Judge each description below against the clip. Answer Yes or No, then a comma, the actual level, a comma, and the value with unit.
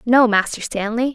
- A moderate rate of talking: Yes, average, 160 wpm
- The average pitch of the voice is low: No, high, 230 Hz